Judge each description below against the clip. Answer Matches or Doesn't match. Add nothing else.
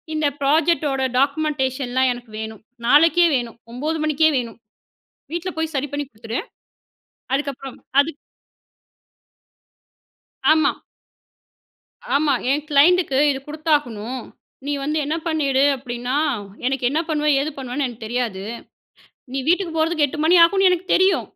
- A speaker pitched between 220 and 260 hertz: Doesn't match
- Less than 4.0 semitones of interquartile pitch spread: Matches